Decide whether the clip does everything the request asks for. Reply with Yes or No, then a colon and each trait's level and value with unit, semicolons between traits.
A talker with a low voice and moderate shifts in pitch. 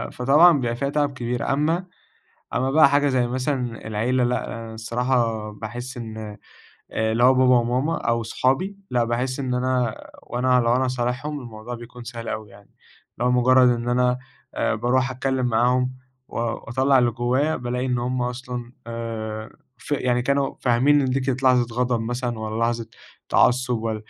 No: low, 125 Hz; narrow, 1.8 semitones